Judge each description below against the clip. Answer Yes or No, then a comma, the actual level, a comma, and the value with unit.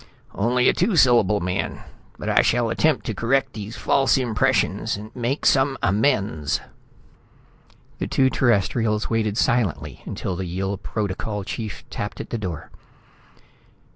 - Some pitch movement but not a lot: Yes, average, 4.2 semitones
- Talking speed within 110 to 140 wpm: Yes, slow, 135 wpm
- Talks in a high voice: No, low, 110 Hz